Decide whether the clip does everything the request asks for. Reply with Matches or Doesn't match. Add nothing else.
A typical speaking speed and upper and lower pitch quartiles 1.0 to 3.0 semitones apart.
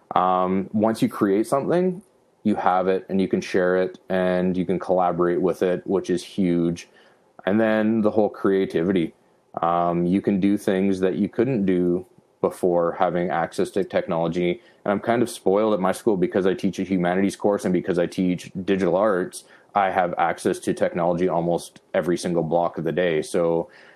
Matches